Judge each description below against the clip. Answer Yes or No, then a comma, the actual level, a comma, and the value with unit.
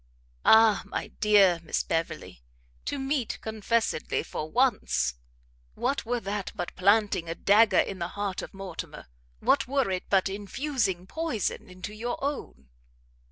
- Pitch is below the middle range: No, high, 205 Hz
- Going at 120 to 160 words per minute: Yes, average, 140 wpm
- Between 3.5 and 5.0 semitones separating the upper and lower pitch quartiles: Yes, average, 4.5 semitones